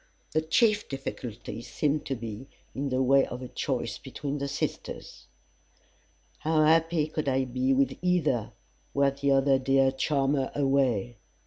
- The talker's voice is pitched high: No, low, 135 Hz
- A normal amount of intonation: No, narrow, 2.2 semitones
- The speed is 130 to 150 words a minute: Yes, average, 140 wpm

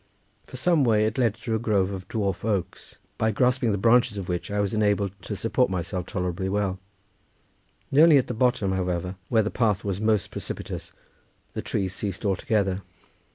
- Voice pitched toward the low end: Yes, low, 105 Hz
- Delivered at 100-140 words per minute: No, average, 180 wpm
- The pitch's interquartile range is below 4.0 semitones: Yes, average, 3.1 semitones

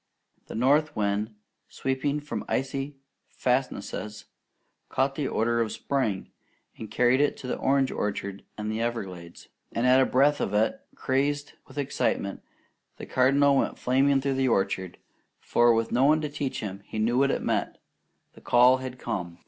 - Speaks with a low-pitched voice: Yes, low, 125 Hz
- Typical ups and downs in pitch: Yes, average, 4.0 semitones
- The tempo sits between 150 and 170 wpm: Yes, average, 165 wpm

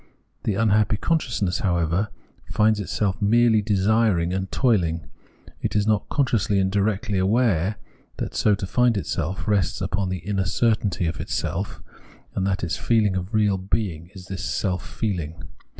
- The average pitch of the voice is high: No, low, 100 Hz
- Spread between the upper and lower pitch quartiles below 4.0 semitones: Yes, average, 2.7 semitones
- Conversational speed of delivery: Yes, average, 165 wpm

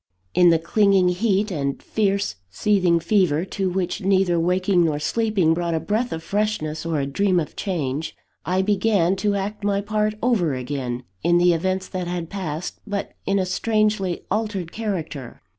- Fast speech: No, average, 170 wpm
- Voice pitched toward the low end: No, medium, 185 Hz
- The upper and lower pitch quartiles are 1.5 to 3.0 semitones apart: No, average, 3.6 semitones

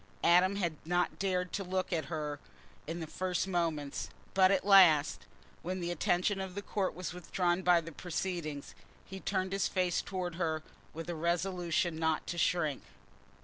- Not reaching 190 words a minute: Yes, average, 170 wpm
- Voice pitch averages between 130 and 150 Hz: No, medium, 175 Hz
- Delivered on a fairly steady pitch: Yes, narrow, 2.3 semitones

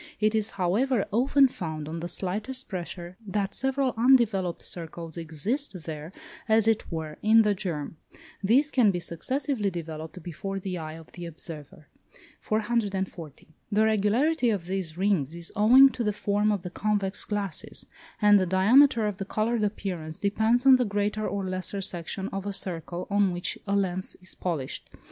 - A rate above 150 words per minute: Yes, average, 165 wpm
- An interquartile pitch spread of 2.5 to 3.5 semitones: No, average, 4.1 semitones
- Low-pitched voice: No, high, 195 Hz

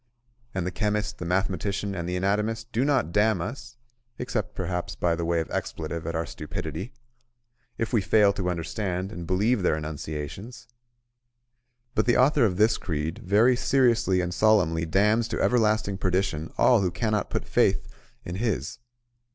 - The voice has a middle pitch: No, very low, 95 Hz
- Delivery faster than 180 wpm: No, average, 160 wpm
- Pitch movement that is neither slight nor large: Yes, average, 4.2 semitones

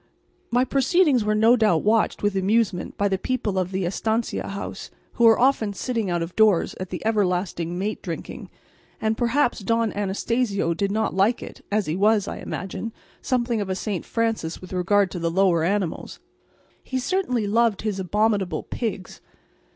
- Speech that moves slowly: No, average, 175 wpm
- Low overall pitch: No, high, 205 Hz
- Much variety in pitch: No, average, 3.5 semitones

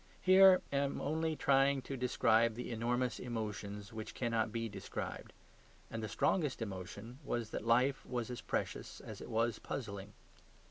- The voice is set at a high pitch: No, low, 120 Hz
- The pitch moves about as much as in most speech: Yes, average, 3.6 semitones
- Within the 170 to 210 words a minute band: No, average, 155 wpm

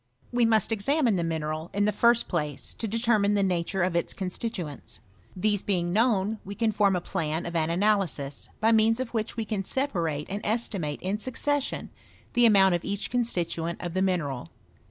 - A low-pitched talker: No, high, 200 Hz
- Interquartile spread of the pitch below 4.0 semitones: No, average, 4.7 semitones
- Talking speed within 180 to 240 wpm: Yes, average, 185 wpm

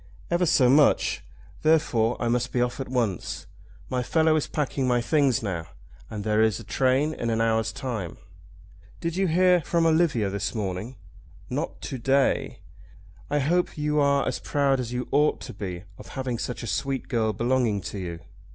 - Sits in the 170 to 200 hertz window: No, low, 125 Hz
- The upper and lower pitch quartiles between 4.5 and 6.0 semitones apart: Yes, average, 4.8 semitones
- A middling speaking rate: Yes, average, 180 wpm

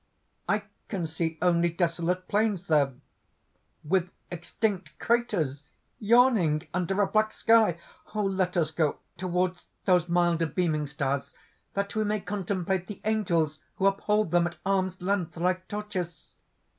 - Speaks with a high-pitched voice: No, medium, 180 Hz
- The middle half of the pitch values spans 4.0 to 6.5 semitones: No, average, 3.2 semitones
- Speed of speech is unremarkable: No, slow, 130 wpm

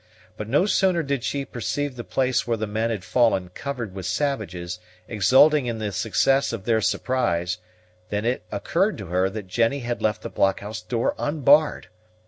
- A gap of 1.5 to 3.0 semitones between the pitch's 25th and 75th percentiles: No, average, 5.2 semitones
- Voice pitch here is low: Yes, low, 115 Hz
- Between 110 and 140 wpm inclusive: No, average, 175 wpm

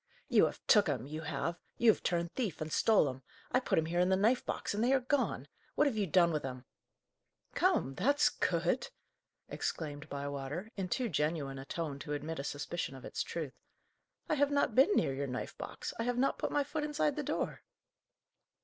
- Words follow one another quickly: Yes, fast, 210 wpm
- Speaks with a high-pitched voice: No, medium, 170 Hz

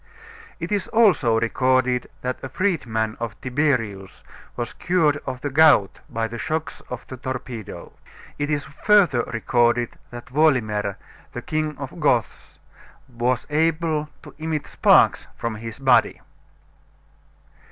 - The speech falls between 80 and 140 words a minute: Yes, slow, 135 wpm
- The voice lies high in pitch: No, low, 130 Hz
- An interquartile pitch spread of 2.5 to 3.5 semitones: No, average, 4.8 semitones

